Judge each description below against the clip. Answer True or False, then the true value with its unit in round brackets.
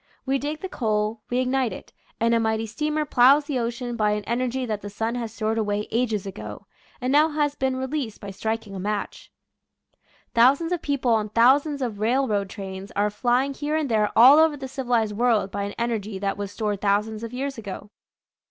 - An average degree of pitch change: True (4.0 semitones)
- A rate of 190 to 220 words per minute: True (200 wpm)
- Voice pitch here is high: True (230 Hz)